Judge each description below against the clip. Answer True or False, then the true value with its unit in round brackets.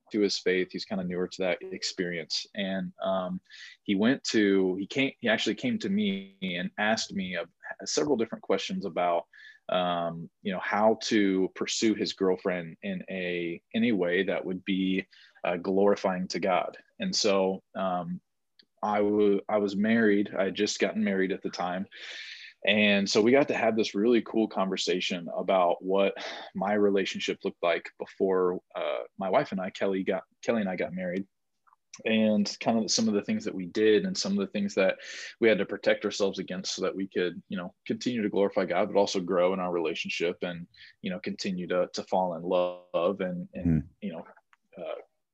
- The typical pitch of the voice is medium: False (100 Hz)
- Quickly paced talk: False (195 wpm)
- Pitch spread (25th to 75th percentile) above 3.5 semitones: False (3.2 semitones)